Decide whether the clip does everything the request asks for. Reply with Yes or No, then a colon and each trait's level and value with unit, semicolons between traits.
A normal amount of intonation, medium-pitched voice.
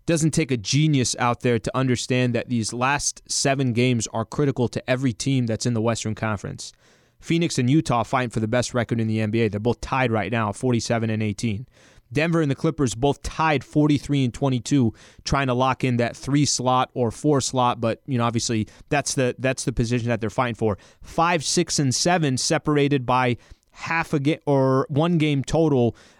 No: average, 3.5 semitones; low, 125 Hz